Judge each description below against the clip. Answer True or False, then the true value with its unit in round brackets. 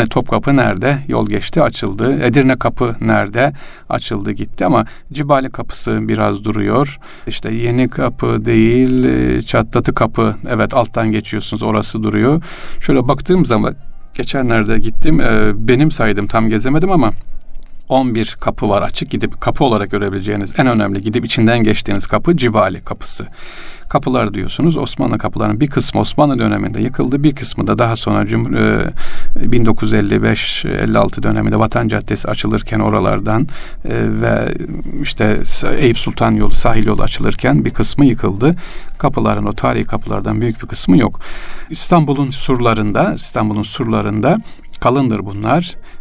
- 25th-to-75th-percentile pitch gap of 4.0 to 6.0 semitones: False (3.5 semitones)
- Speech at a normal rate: True (130 wpm)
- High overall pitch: False (115 Hz)